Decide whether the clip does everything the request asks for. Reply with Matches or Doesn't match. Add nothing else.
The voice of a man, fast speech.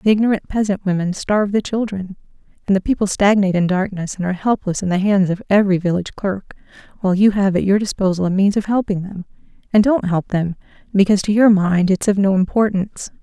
Doesn't match